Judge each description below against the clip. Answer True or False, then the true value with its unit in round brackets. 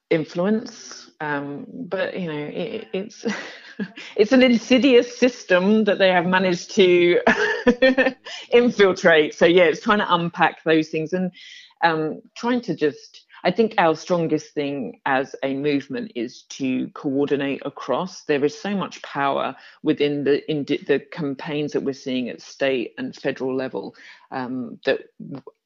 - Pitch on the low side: False (180 Hz)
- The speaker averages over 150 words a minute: False (145 wpm)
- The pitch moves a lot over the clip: True (8.0 semitones)